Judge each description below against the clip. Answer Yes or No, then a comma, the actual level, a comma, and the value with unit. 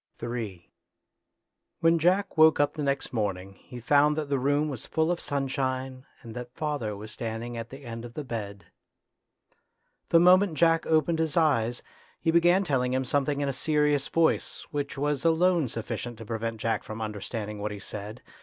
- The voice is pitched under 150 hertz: Yes, low, 135 Hz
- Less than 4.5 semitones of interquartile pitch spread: No, average, 5.3 semitones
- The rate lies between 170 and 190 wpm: Yes, average, 180 wpm